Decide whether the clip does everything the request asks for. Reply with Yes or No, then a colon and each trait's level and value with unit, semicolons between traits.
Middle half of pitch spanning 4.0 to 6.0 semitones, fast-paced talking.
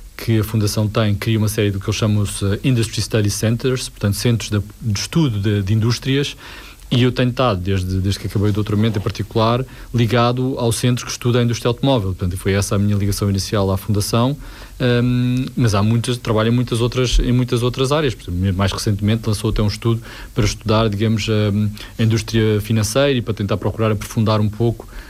No: average, 2.7 semitones; fast, 195 wpm